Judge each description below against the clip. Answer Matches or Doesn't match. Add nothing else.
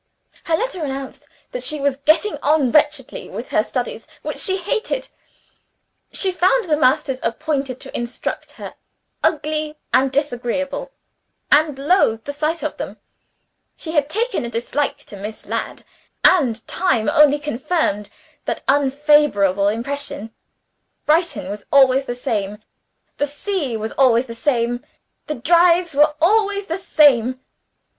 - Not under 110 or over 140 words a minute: Matches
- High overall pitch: Matches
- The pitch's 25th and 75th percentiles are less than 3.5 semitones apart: Doesn't match